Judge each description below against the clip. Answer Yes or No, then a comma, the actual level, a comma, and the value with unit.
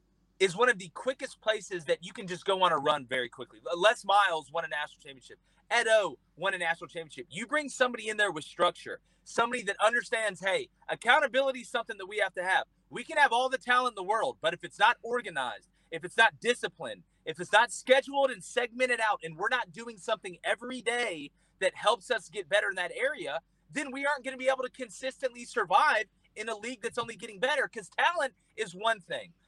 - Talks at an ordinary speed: No, fast, 220 wpm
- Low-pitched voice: No, high, 225 Hz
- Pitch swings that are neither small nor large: No, wide, 5.8 semitones